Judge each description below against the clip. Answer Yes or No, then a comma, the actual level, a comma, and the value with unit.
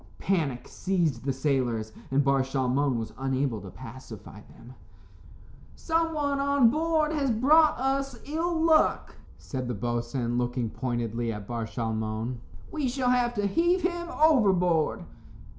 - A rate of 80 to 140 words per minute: Yes, slow, 135 wpm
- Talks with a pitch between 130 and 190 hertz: Yes, medium, 140 Hz